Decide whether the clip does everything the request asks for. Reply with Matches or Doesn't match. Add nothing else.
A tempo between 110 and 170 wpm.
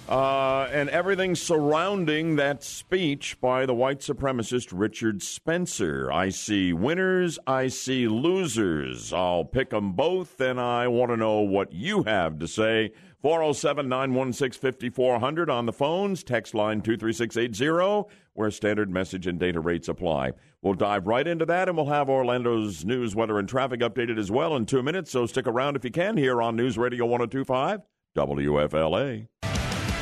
Matches